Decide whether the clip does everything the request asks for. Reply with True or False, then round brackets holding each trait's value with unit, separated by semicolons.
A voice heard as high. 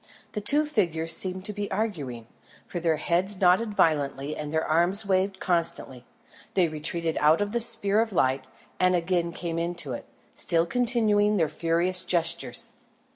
False (175 Hz)